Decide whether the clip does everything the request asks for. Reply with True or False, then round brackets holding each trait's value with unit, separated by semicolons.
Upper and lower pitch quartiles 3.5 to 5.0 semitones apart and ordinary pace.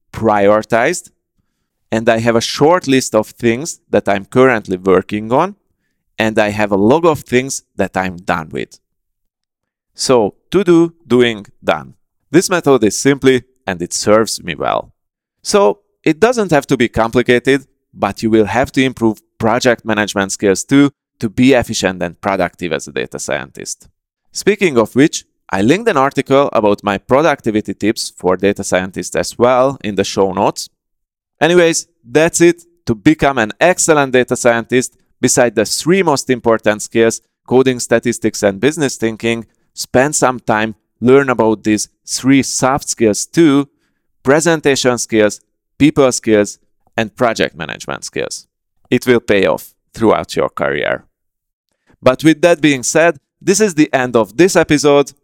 True (4.7 semitones; 155 wpm)